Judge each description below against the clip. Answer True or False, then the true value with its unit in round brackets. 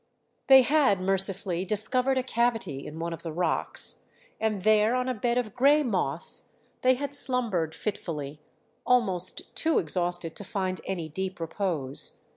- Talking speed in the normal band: True (150 wpm)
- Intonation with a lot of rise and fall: True (6.5 semitones)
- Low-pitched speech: False (195 Hz)